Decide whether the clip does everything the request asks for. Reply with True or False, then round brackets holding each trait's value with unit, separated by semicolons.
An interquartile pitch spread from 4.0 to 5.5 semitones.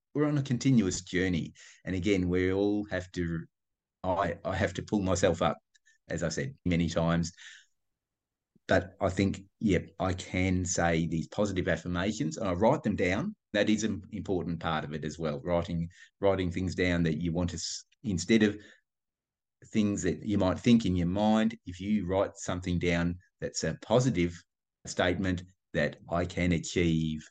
False (3.2 semitones)